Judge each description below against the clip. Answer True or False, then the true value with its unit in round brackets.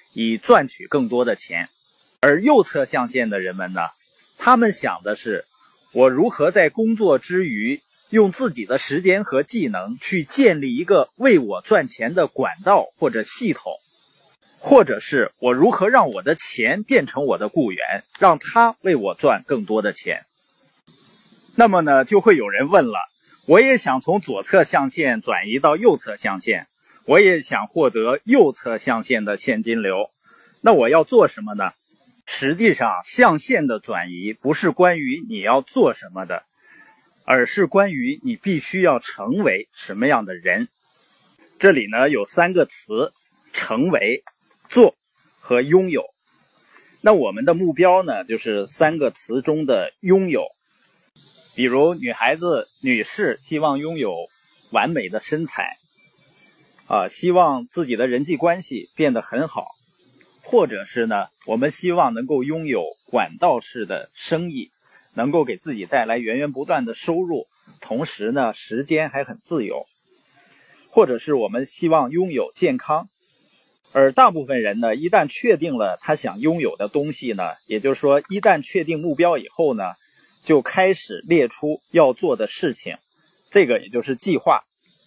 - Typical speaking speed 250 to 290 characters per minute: False (225 characters per minute)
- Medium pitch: True (175 Hz)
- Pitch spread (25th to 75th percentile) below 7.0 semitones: False (8.4 semitones)